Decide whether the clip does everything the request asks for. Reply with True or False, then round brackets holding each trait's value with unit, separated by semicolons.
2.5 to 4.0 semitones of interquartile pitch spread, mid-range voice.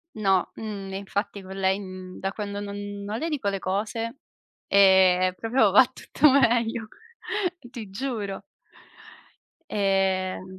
False (2.9 semitones; 200 Hz)